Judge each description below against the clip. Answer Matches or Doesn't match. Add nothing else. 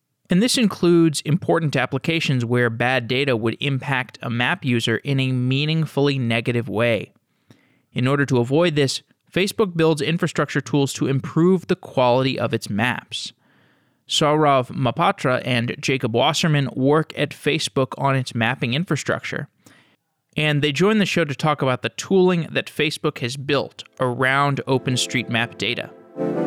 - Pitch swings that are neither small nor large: Matches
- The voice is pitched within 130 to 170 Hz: Matches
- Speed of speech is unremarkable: Matches